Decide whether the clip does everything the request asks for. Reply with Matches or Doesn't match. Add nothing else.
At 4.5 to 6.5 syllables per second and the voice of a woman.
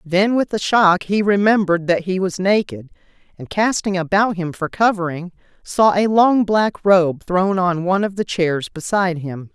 Matches